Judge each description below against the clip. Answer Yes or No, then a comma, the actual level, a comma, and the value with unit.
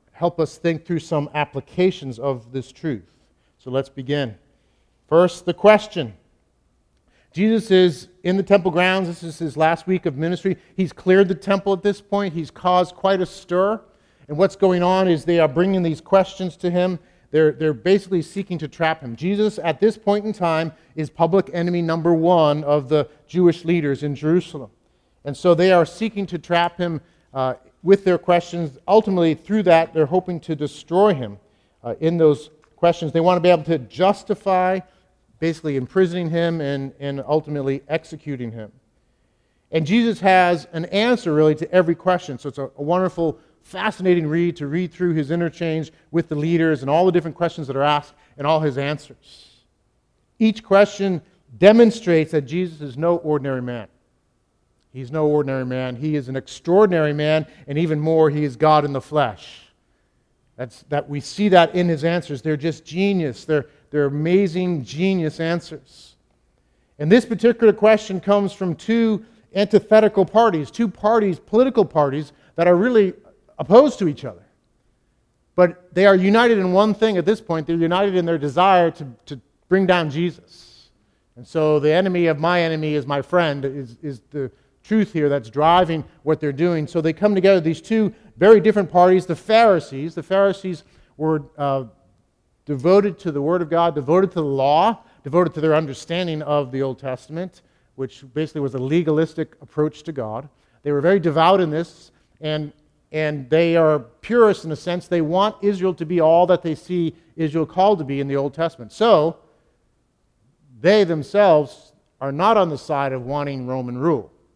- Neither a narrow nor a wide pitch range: Yes, average, 3.9 semitones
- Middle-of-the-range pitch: Yes, medium, 165 Hz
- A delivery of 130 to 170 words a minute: No, average, 180 wpm